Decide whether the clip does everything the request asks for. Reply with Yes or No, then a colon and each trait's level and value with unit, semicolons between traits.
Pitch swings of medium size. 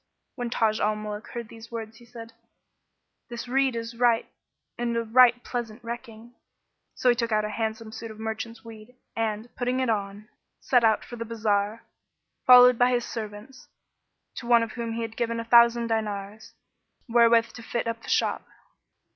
No: narrow, 1.5 semitones